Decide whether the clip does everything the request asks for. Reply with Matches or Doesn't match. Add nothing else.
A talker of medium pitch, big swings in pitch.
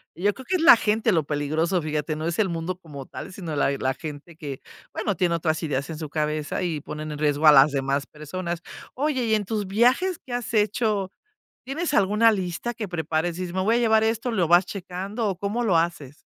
Matches